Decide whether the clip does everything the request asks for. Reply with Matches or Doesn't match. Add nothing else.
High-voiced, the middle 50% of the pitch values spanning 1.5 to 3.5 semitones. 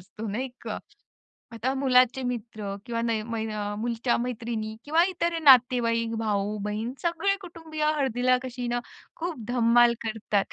Matches